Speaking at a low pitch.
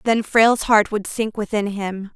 No: high, 210 Hz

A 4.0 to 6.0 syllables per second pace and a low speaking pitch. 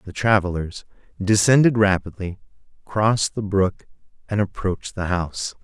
Yes: 5.0 syllables/s; very low, 95 Hz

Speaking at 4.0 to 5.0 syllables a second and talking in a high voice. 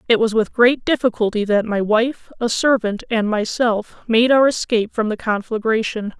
Yes: 4.8 syllables/s; high, 225 Hz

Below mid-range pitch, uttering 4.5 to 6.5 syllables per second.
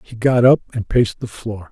Yes: low, 115 Hz; 5.4 syllables/s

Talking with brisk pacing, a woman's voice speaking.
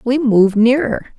No: average, 150 wpm; female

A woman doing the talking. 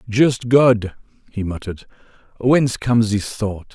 No: male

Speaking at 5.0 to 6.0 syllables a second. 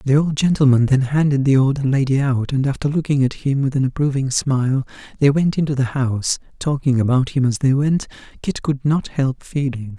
Yes: 5.3 syllables/s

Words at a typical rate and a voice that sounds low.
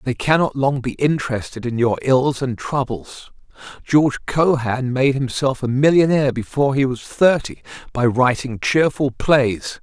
Yes: average, 145 wpm; low, 130 Hz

